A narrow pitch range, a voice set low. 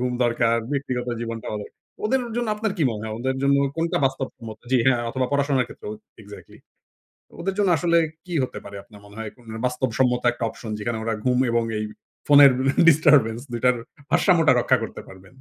No: average, 3.7 semitones; low, 125 Hz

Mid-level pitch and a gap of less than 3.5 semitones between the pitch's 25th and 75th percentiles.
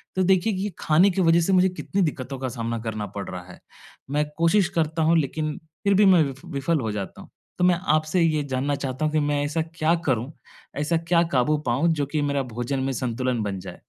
No: medium, 150 Hz; average, 4.6 semitones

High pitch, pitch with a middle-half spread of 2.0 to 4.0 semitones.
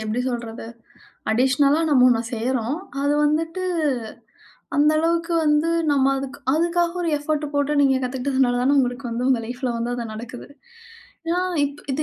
Yes: very high, 275 Hz; average, 3.4 semitones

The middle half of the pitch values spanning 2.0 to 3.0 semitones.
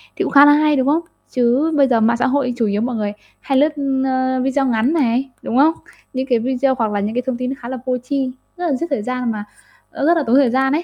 Yes: average, 2.7 semitones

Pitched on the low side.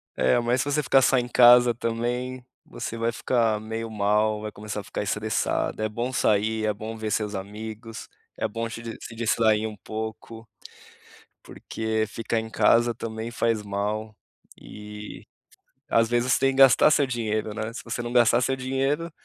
Yes: low, 115 Hz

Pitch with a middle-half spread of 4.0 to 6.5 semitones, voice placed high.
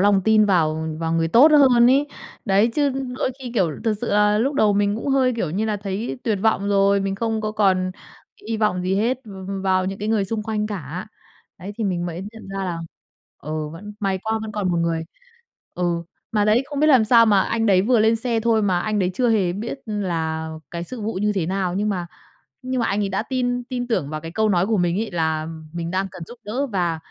No: average, 3.6 semitones; high, 205 Hz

